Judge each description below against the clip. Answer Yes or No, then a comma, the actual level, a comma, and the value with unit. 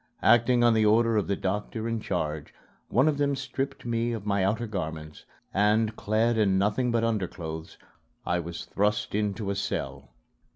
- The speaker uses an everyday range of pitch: Yes, average, 3.5 semitones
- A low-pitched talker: Yes, low, 105 Hz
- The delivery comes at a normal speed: Yes, average, 170 wpm